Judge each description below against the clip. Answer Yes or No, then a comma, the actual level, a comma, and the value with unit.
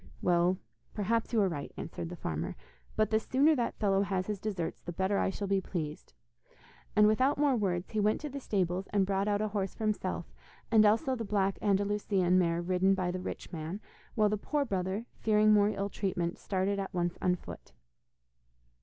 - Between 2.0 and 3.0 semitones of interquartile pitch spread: Yes, average, 2.7 semitones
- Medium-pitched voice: No, high, 195 Hz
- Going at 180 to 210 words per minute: Yes, average, 200 wpm